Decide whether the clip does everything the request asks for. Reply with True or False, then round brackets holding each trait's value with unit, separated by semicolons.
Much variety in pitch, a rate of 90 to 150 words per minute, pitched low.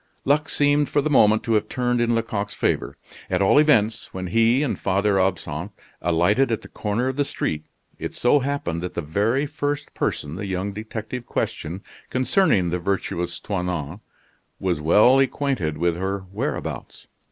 False (6.0 semitones; 165 wpm; 105 Hz)